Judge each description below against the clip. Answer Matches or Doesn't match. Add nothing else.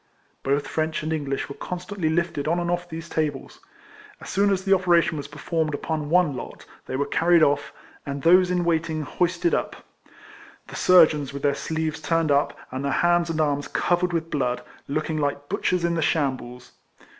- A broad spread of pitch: Doesn't match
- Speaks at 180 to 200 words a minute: Matches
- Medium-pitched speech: Matches